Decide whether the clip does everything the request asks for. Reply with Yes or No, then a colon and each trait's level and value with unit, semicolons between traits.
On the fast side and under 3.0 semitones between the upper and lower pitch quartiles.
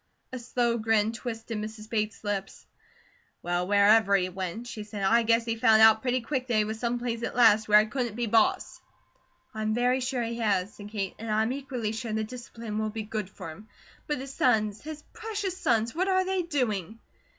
Yes: fast, 210 wpm; narrow, 2.4 semitones